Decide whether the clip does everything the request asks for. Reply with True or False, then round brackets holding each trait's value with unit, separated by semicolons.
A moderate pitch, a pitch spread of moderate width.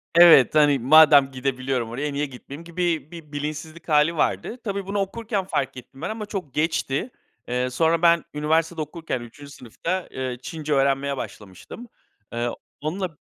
True (150 Hz; 3.8 semitones)